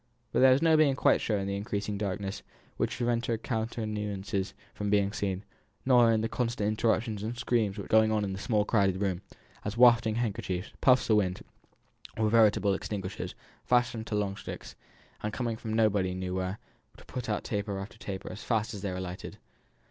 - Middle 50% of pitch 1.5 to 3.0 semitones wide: Yes, average, 2.7 semitones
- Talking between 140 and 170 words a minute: No, average, 190 wpm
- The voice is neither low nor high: No, low, 105 Hz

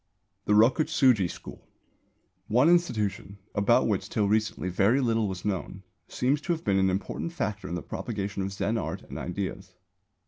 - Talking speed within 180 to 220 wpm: No, average, 165 wpm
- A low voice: Yes, low, 105 Hz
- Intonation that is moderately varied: Yes, average, 4.3 semitones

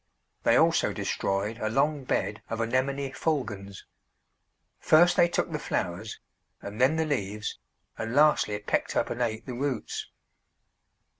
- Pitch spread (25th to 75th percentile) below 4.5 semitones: No, average, 5.1 semitones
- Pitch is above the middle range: No, low, 125 Hz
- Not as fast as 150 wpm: Yes, average, 140 wpm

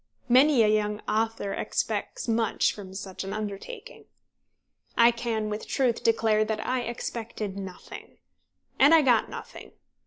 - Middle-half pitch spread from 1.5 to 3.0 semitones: Yes, narrow, 2.4 semitones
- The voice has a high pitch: Yes, high, 225 Hz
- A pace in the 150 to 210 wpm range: No, slow, 135 wpm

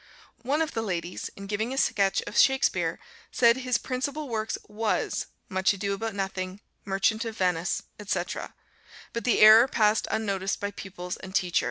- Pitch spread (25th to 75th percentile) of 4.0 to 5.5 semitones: No, average, 3.3 semitones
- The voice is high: Yes, high, 210 Hz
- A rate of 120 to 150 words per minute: No, average, 165 wpm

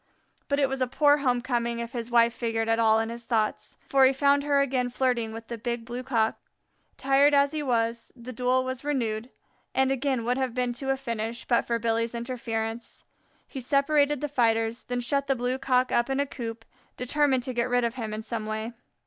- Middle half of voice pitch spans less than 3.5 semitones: Yes, narrow, 2.6 semitones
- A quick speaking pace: Yes, fast, 215 wpm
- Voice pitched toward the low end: No, high, 245 Hz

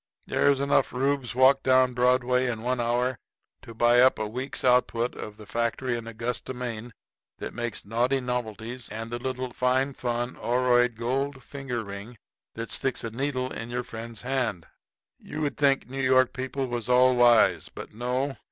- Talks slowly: No, average, 170 wpm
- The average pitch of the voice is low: Yes, low, 125 Hz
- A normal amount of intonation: No, narrow, 1.8 semitones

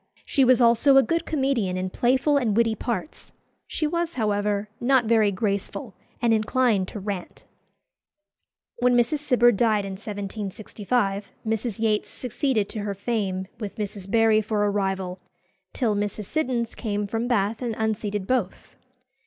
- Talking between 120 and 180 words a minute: Yes, average, 150 wpm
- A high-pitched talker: Yes, high, 220 Hz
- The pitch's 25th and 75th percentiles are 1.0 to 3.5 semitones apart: Yes, average, 3.2 semitones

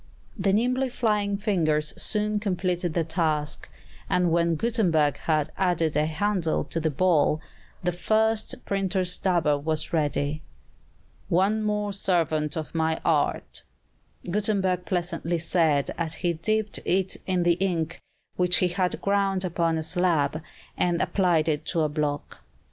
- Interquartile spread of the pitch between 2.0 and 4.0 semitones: Yes, average, 3.6 semitones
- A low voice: No, medium, 175 Hz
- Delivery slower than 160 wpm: Yes, average, 140 wpm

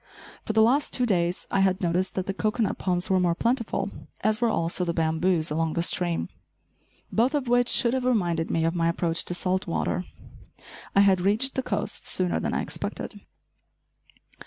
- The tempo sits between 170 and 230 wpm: Yes, average, 185 wpm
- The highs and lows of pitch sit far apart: No, average, 4.5 semitones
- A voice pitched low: No, medium, 185 Hz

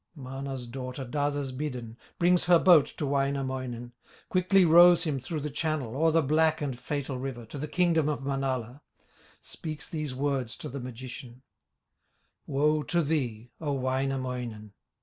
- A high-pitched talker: No, medium, 140 Hz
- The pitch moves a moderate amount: Yes, average, 3.2 semitones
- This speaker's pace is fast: No, average, 150 wpm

